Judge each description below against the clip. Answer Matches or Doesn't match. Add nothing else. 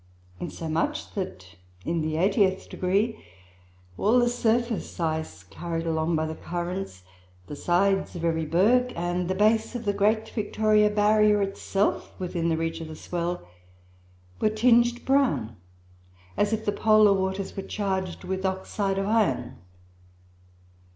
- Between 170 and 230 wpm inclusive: Doesn't match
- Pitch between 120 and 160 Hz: Doesn't match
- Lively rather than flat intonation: Doesn't match